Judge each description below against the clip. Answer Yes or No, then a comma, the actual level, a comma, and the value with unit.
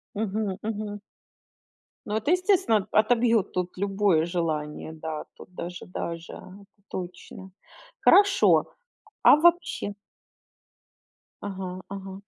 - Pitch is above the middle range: Yes, high, 195 Hz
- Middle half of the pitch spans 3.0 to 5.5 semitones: Yes, average, 3.6 semitones